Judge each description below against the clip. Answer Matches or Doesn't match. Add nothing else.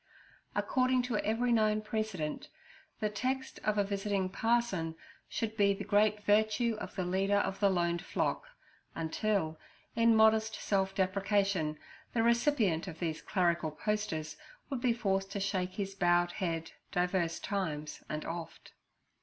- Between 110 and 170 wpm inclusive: Matches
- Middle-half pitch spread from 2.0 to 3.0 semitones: Doesn't match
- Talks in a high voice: Matches